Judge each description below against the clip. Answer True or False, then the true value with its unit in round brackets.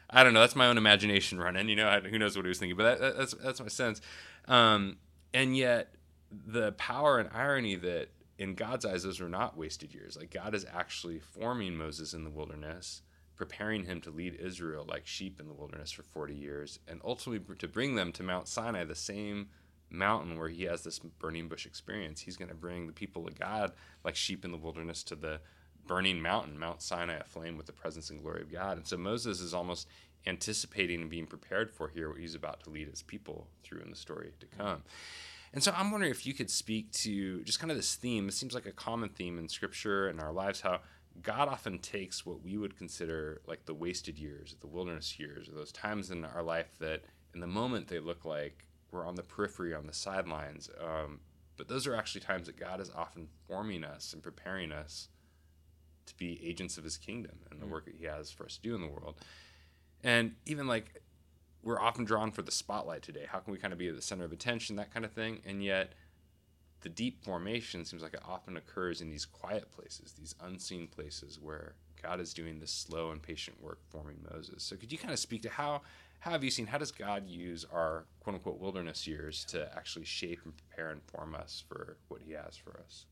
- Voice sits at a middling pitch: False (85 Hz)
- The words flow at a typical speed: False (225 wpm)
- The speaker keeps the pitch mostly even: False (4.6 semitones)